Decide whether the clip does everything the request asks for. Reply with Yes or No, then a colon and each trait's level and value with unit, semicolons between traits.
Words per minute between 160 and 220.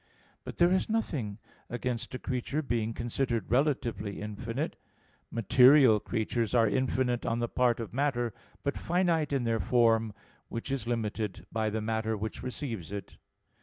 No: average, 150 wpm